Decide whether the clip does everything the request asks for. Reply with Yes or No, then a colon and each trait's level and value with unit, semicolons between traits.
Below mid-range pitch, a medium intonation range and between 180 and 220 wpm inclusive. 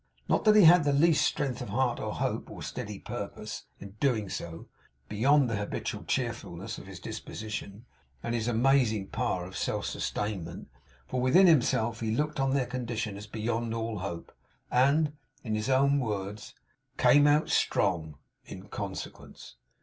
No: low, 115 Hz; average, 4.9 semitones; average, 160 wpm